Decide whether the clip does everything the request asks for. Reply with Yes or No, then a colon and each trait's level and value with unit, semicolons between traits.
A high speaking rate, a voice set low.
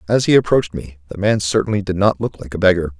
Yes: fast, 260 wpm; very low, 95 Hz